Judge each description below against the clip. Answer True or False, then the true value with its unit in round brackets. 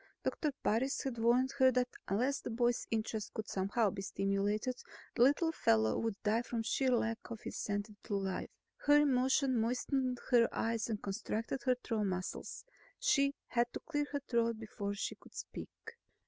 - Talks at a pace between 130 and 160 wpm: False (170 wpm)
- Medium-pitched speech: False (230 Hz)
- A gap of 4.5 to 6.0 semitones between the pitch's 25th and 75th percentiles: False (3.6 semitones)